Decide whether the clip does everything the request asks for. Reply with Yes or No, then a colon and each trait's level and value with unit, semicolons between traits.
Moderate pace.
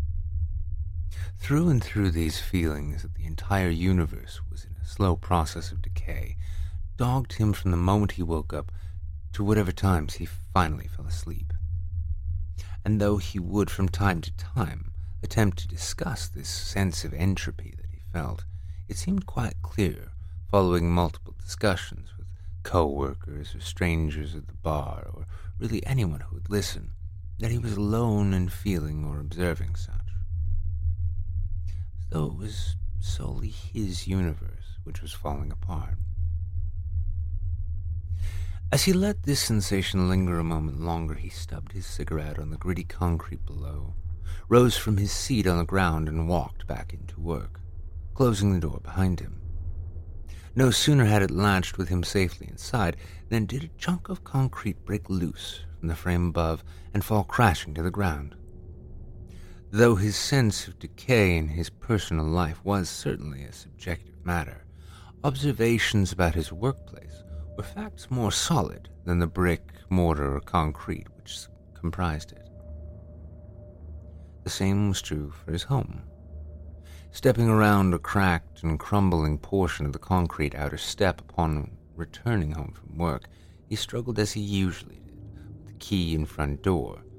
Yes: average, 150 wpm